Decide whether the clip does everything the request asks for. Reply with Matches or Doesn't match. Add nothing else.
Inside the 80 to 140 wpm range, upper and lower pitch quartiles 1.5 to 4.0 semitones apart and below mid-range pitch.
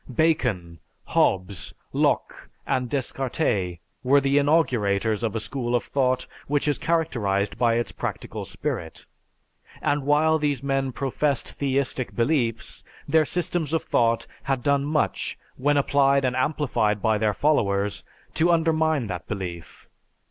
Doesn't match